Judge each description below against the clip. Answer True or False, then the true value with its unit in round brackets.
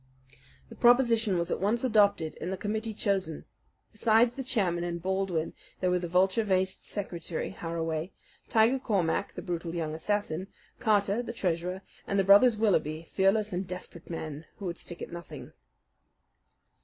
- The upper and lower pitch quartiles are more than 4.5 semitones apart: False (3.9 semitones)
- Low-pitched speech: False (190 Hz)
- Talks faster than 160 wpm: False (155 wpm)